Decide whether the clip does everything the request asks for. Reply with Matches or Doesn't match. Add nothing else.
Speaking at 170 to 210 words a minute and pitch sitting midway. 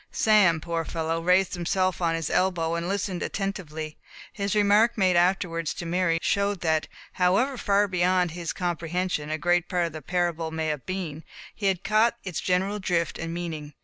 Matches